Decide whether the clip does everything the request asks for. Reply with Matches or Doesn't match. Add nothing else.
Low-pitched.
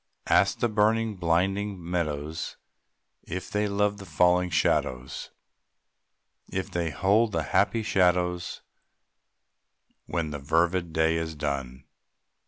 Matches